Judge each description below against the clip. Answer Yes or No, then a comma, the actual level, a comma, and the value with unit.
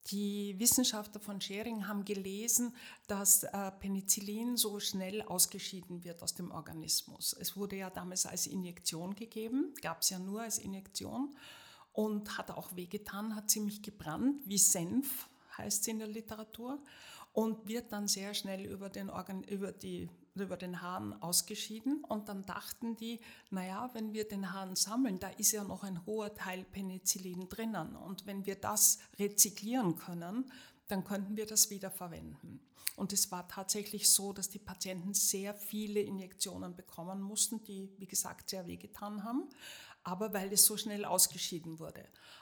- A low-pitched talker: No, high, 200 Hz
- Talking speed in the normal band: Yes, average, 155 wpm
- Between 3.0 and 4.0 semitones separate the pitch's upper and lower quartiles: No, narrow, 2.4 semitones